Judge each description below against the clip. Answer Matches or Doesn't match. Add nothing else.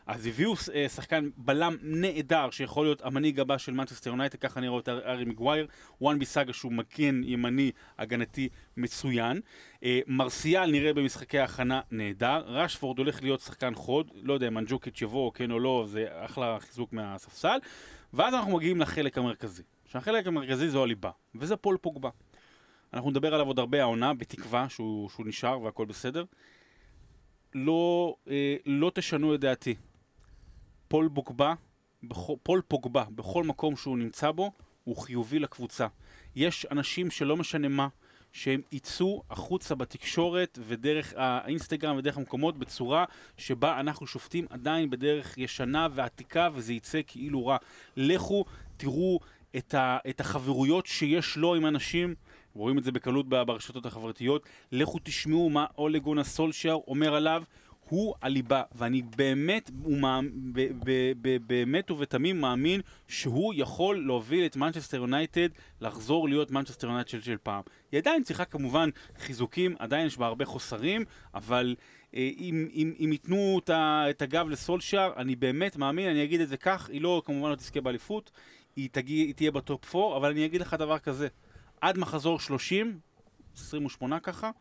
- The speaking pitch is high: Doesn't match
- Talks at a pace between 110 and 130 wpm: Doesn't match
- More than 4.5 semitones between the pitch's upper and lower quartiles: Doesn't match